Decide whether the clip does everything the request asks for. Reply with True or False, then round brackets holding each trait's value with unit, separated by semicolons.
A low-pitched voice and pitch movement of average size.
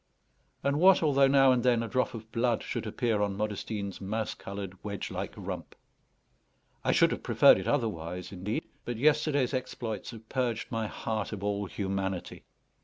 True (110 Hz; 4.0 semitones)